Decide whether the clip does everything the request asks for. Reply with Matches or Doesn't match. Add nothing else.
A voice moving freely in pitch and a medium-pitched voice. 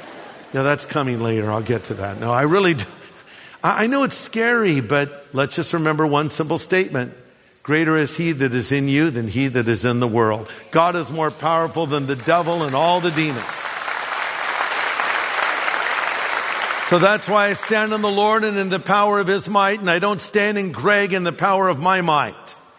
Matches